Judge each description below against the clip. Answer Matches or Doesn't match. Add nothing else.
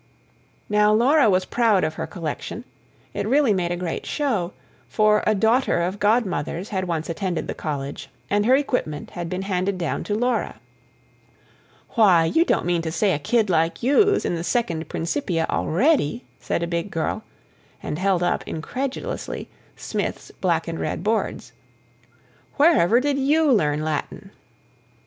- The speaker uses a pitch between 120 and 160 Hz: Doesn't match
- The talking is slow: Doesn't match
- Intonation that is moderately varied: Doesn't match